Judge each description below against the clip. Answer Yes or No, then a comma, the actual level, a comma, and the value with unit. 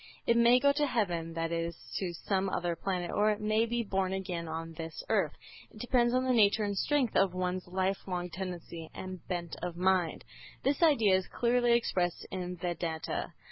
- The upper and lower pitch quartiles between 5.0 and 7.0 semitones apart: No, average, 4.5 semitones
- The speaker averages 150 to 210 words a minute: Yes, average, 190 wpm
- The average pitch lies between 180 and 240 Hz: Yes, high, 190 Hz